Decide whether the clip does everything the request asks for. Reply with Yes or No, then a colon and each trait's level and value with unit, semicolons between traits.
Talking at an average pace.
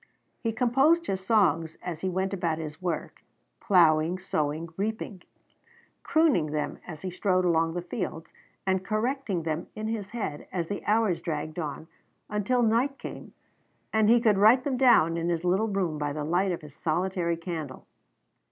Yes: average, 170 wpm